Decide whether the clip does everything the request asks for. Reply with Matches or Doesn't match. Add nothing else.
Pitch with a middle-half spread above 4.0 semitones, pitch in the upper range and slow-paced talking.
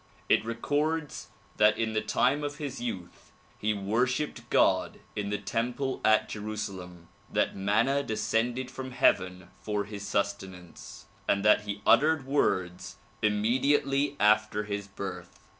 Doesn't match